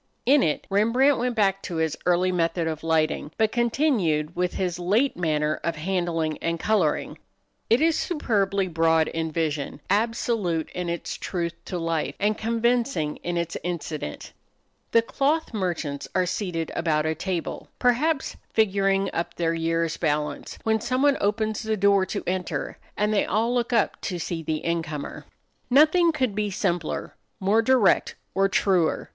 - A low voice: No, medium, 185 Hz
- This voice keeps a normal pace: Yes, average, 155 wpm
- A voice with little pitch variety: No, average, 5.2 semitones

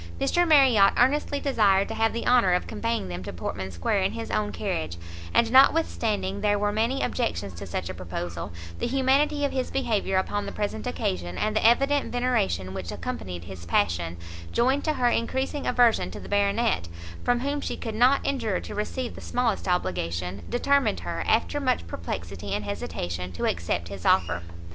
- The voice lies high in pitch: Yes, high, 205 Hz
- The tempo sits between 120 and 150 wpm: No, average, 180 wpm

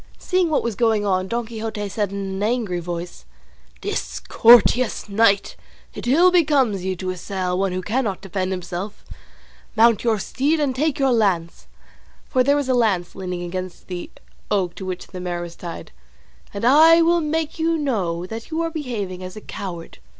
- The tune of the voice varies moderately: No, wide, 5.9 semitones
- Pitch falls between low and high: No, high, 210 Hz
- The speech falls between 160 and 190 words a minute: Yes, average, 180 wpm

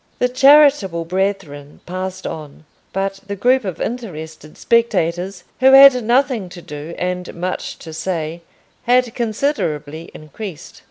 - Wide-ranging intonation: Yes, wide, 6.6 semitones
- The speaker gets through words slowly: Yes, slow, 125 wpm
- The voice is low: No, high, 190 Hz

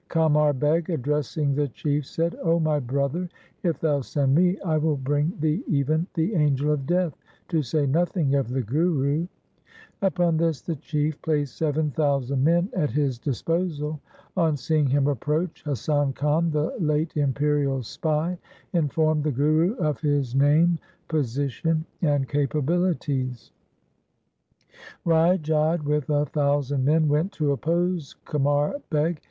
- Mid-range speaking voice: Yes, medium, 150 Hz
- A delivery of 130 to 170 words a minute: Yes, average, 145 wpm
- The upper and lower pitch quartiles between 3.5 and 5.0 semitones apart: No, narrow, 2.4 semitones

